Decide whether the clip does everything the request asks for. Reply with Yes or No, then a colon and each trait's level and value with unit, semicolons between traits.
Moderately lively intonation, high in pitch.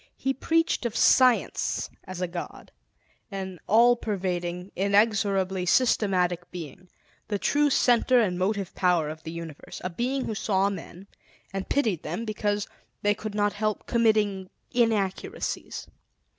Yes: average, 3.6 semitones; high, 200 Hz